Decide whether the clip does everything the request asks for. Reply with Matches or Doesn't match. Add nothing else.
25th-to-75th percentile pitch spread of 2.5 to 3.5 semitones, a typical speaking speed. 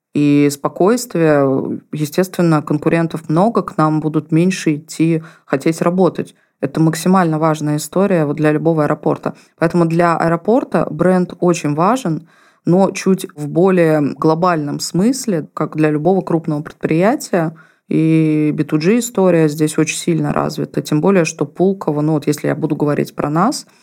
Matches